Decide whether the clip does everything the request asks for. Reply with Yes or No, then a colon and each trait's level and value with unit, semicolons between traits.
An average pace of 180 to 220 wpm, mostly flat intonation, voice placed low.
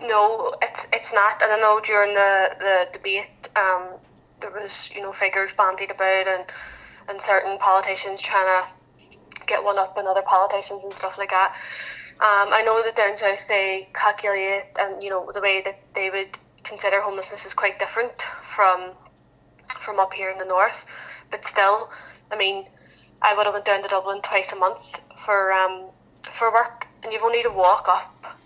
No: average, 185 wpm; narrow, 1.5 semitones; high, 200 Hz